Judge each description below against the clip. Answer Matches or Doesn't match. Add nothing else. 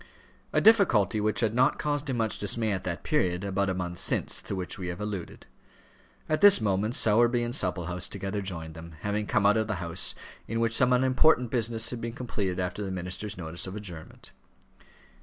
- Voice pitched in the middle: Doesn't match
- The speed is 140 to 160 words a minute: Doesn't match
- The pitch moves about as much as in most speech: Matches